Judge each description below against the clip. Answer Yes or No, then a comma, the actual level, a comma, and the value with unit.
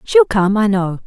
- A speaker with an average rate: No, fast, 225 wpm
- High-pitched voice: Yes, high, 215 Hz